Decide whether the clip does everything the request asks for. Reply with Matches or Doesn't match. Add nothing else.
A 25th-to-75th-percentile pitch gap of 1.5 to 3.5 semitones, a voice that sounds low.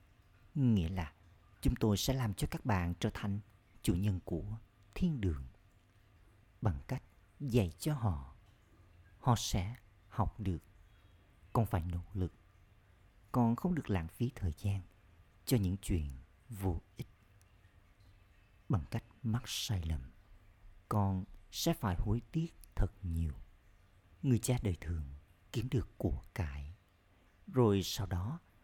Matches